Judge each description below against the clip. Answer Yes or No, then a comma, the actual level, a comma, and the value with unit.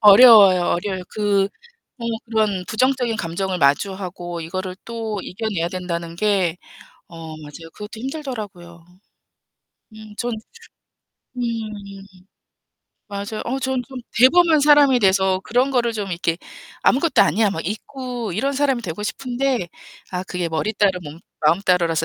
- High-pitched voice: Yes, high, 205 Hz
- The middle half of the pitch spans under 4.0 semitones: No, average, 5.3 semitones